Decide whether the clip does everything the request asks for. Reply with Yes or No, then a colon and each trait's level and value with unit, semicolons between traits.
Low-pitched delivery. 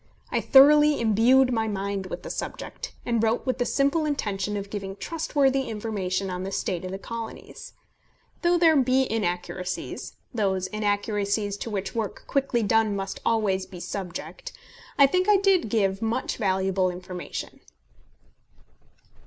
No: high, 215 Hz